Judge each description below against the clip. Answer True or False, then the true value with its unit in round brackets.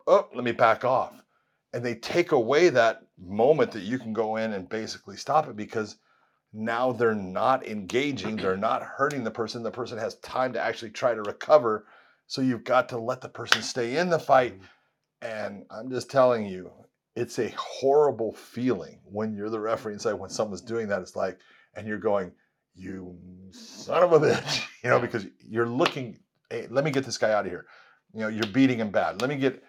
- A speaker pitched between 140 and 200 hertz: False (115 Hz)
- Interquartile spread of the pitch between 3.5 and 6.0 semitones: False (3.0 semitones)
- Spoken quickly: True (210 wpm)